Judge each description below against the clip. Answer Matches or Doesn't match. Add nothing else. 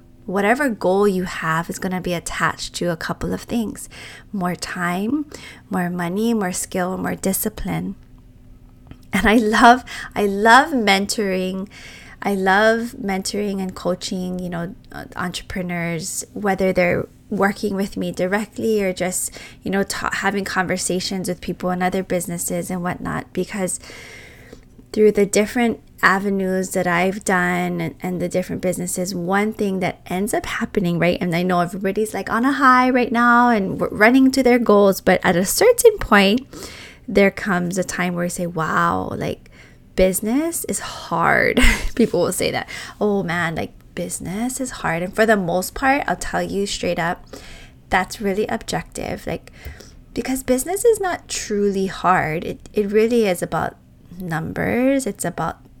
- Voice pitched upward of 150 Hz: Matches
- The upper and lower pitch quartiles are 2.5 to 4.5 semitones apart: Matches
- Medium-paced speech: Matches